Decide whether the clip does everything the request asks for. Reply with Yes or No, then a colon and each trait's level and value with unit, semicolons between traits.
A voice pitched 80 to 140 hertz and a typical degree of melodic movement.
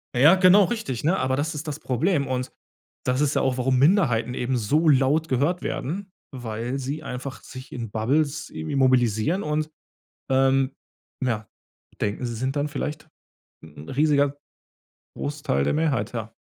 Yes: low, 135 Hz; average, 3.6 semitones